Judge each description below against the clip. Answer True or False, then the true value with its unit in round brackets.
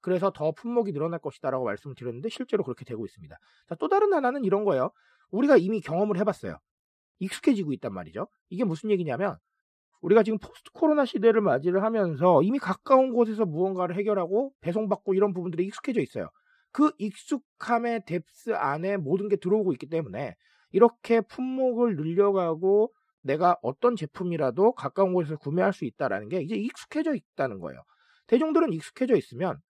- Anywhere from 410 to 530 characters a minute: True (415 characters per minute)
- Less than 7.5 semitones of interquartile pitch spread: True (5.1 semitones)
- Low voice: False (205 Hz)